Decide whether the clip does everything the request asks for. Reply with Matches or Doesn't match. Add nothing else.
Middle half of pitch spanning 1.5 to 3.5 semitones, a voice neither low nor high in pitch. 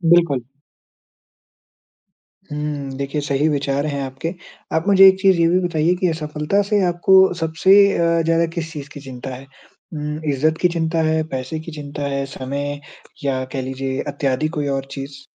Matches